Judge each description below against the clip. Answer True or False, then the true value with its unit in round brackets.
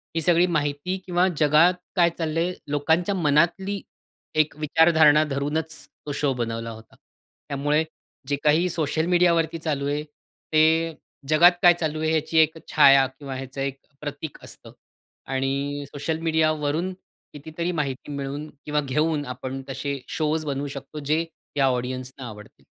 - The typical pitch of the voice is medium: True (150 Hz)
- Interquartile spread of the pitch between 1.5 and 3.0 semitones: True (2.6 semitones)